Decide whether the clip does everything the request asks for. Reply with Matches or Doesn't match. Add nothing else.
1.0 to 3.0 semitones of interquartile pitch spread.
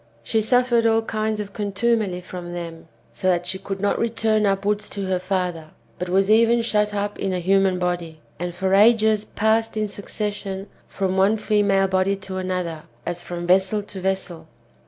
Matches